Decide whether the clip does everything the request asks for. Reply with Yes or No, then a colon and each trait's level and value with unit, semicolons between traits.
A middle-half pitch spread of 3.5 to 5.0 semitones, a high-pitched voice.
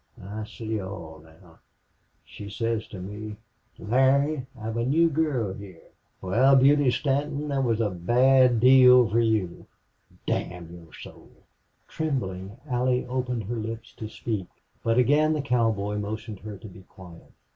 No: average, 4.5 semitones; low, 115 Hz